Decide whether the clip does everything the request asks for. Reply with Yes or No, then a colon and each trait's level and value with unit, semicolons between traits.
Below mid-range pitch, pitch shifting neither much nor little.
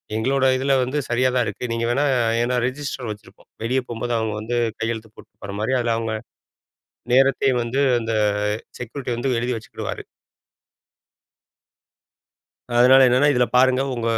No: low, 125 Hz; narrow, 2.2 semitones